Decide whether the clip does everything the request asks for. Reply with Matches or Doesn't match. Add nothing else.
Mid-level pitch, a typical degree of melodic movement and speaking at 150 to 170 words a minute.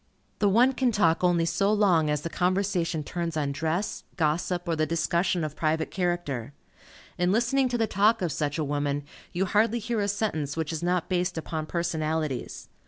Doesn't match